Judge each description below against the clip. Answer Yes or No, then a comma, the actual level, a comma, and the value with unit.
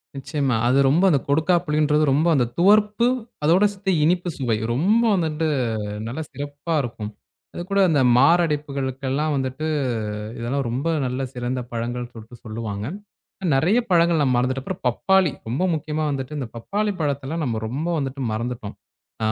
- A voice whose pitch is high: No, medium, 140 Hz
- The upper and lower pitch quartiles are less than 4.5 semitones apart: No, average, 4.8 semitones